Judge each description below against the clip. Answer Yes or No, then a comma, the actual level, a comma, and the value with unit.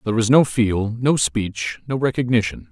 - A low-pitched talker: Yes, low, 115 Hz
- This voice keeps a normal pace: Yes, average, 175 wpm